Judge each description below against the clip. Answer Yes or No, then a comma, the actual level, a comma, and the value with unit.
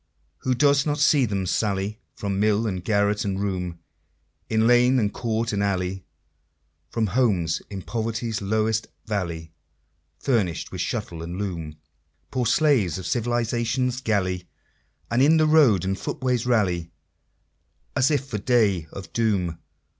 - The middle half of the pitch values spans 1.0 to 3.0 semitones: No, average, 4.4 semitones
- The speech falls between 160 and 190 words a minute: No, average, 145 wpm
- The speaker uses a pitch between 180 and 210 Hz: No, low, 105 Hz